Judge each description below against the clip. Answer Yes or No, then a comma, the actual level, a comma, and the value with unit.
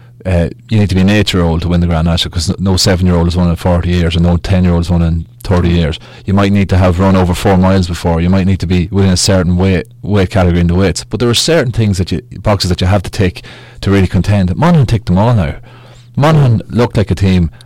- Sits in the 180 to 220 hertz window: No, very low, 95 Hz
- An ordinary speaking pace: No, fast, 285 wpm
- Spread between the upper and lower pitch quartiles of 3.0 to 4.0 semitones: Yes, average, 3.6 semitones